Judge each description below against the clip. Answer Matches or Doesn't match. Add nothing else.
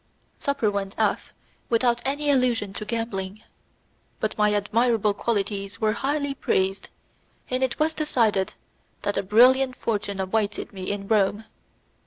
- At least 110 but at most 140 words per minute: Matches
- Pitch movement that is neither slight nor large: Matches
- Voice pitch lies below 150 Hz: Doesn't match